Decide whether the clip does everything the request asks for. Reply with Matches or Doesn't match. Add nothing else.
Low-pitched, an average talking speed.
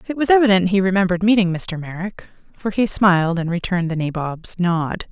Doesn't match